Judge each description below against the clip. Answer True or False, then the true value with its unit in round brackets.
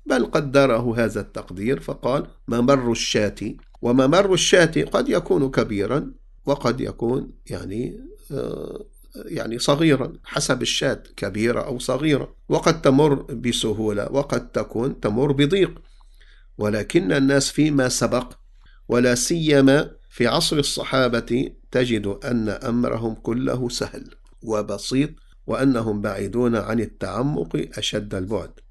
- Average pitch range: True (3.4 semitones)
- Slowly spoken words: True (105 wpm)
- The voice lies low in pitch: True (125 Hz)